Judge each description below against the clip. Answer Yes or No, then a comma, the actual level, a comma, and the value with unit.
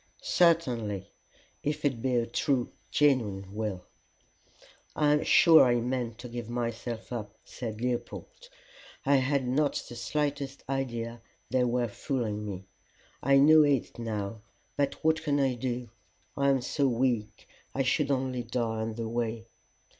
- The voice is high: No, low, 125 Hz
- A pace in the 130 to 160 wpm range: Yes, average, 145 wpm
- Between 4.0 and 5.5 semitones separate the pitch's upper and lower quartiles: No, average, 3.3 semitones